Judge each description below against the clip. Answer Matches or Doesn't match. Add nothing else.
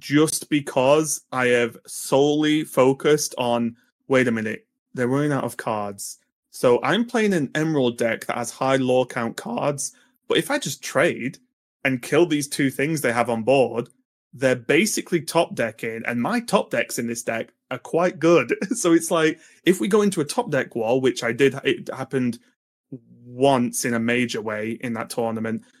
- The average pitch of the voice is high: Doesn't match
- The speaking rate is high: Doesn't match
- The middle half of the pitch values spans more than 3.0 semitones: Matches